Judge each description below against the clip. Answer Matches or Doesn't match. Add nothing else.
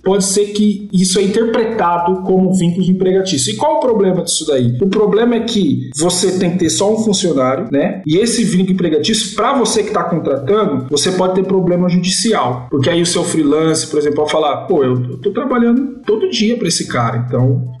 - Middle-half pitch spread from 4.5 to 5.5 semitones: Matches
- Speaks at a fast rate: Matches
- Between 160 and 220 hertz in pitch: Matches